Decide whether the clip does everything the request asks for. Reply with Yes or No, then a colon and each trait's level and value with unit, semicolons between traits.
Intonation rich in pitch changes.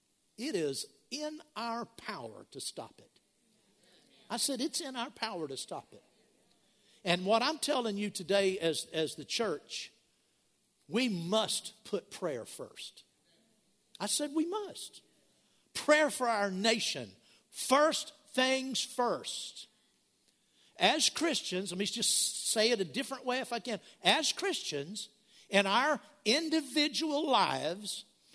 Yes: wide, 6.4 semitones